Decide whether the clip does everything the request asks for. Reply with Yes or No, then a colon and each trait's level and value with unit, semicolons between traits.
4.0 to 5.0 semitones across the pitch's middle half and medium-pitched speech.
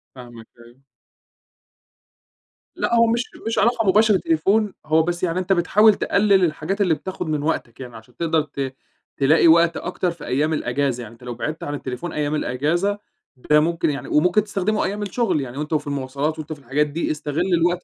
Yes: average, 4.7 semitones; medium, 160 Hz